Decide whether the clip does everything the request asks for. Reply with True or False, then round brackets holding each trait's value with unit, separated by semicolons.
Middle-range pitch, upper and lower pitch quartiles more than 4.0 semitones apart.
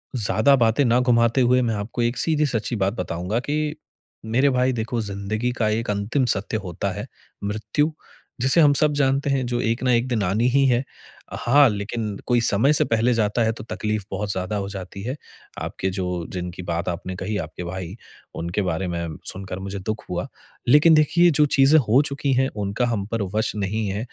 False (110 Hz; 4.5 semitones)